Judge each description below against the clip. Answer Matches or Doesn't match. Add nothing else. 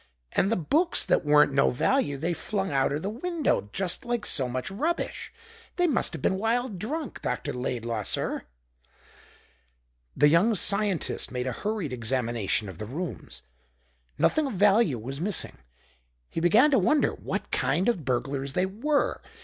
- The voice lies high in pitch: Doesn't match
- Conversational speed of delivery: Matches